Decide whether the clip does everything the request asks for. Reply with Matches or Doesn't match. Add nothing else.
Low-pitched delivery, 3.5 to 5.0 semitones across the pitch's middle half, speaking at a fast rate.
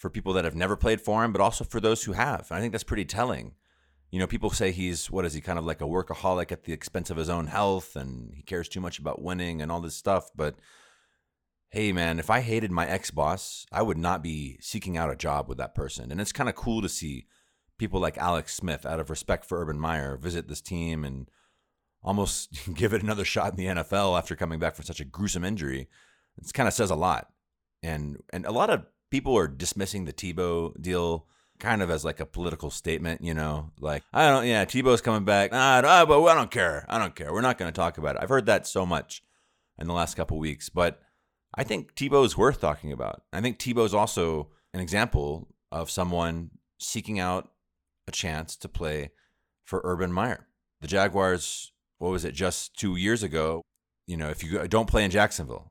Matches